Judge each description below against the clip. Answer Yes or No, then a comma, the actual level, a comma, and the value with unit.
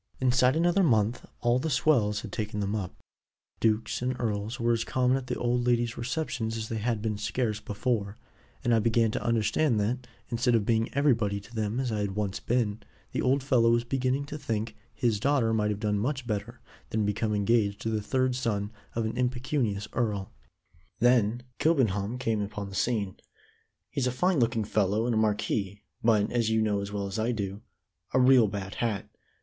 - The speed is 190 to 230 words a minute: Yes, average, 195 wpm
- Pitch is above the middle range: No, low, 115 Hz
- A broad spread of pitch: No, average, 3.1 semitones